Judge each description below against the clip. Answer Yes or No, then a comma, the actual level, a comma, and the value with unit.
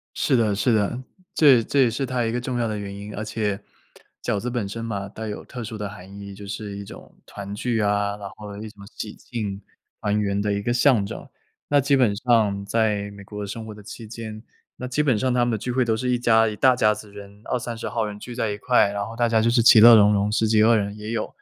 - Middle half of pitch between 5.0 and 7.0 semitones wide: No, average, 2.7 semitones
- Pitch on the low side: Yes, low, 110 Hz